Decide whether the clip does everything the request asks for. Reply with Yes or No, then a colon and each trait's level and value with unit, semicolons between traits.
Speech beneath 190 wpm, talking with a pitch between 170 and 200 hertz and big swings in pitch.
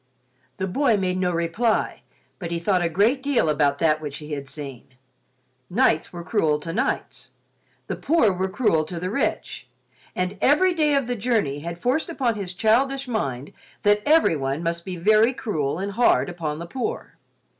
Yes: average, 170 wpm; medium, 185 Hz; wide, 6.9 semitones